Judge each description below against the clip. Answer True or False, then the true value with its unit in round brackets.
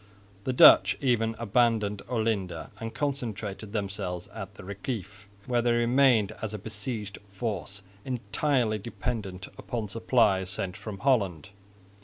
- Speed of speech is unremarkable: False (125 wpm)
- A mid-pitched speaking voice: False (110 Hz)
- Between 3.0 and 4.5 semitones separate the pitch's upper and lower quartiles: True (3.3 semitones)